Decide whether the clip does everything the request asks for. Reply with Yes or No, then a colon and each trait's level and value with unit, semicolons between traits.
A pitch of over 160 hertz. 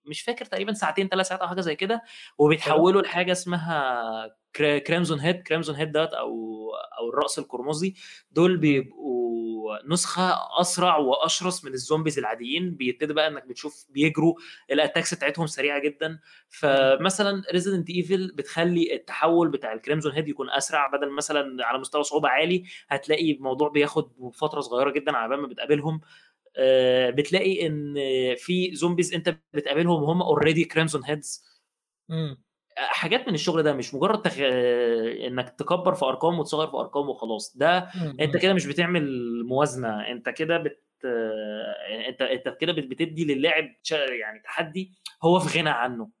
No: medium, 155 Hz